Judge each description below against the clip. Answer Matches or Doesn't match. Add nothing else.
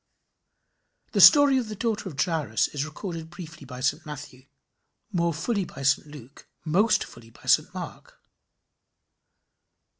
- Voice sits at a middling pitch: Matches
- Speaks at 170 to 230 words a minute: Doesn't match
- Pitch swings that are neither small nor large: Doesn't match